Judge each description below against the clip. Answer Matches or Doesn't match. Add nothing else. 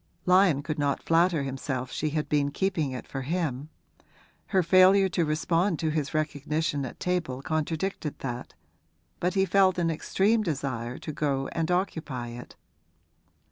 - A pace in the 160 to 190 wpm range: Doesn't match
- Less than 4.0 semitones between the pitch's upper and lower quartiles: Doesn't match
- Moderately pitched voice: Matches